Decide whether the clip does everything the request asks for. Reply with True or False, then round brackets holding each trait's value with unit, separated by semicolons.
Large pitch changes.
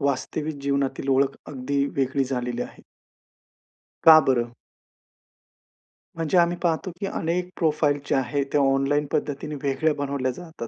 False (2.7 semitones)